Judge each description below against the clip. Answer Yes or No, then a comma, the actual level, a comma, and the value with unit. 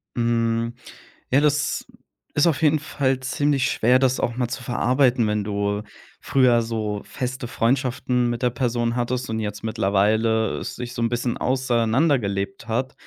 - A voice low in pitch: Yes, low, 120 Hz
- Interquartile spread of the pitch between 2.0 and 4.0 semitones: Yes, narrow, 2.5 semitones